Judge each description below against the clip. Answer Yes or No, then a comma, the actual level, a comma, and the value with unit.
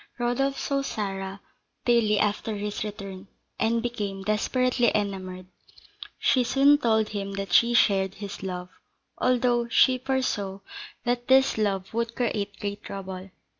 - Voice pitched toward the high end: Yes, high, 210 Hz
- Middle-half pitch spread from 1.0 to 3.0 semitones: No, average, 3.6 semitones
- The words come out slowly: Yes, slow, 130 wpm